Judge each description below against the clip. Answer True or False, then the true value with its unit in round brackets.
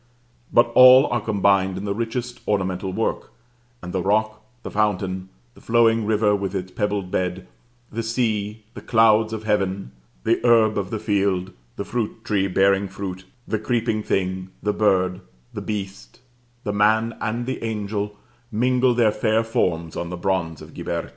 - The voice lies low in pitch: True (105 Hz)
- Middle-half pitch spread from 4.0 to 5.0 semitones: False (2.8 semitones)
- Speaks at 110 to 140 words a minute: False (165 wpm)